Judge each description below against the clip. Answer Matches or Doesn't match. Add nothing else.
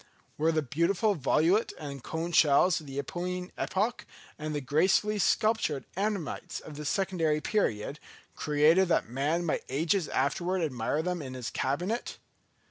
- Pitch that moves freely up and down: Doesn't match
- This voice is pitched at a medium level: Matches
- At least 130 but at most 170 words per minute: Matches